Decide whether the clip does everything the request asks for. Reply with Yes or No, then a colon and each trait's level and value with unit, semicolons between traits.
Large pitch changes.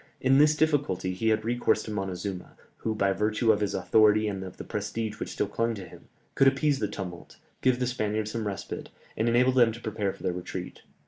No: average, 3.4 semitones